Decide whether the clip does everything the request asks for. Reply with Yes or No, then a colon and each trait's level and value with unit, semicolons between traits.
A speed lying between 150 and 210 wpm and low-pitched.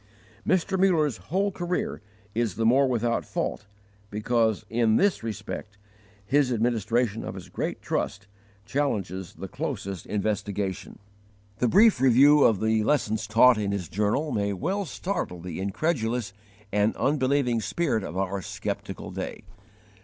No: slow, 135 wpm; low, 115 Hz